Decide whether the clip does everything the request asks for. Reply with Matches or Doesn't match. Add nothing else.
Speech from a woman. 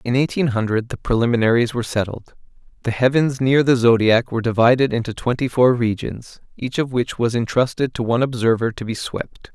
Doesn't match